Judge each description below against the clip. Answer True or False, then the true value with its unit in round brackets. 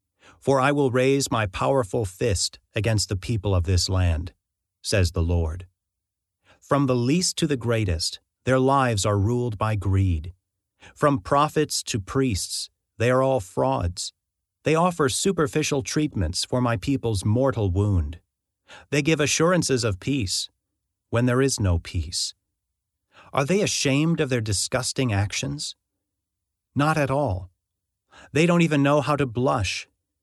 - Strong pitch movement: True (6.4 semitones)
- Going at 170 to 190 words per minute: False (145 wpm)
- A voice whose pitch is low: True (110 Hz)